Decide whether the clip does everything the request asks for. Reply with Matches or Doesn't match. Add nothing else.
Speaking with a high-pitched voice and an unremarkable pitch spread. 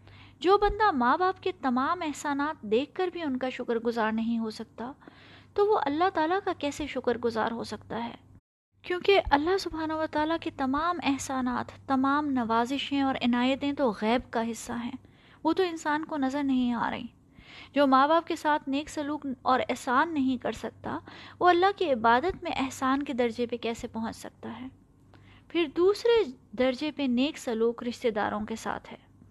Matches